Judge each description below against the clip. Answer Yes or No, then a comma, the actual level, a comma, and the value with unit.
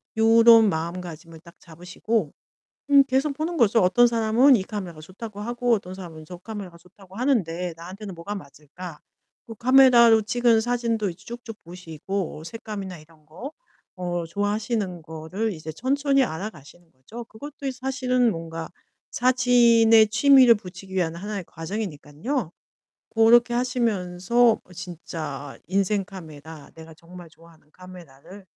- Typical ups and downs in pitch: No, wide, 5.8 semitones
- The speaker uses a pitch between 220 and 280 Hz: No, high, 195 Hz